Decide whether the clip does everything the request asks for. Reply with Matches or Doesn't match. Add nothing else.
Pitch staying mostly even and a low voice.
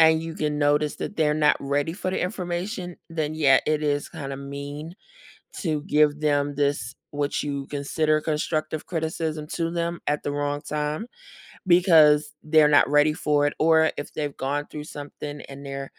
Doesn't match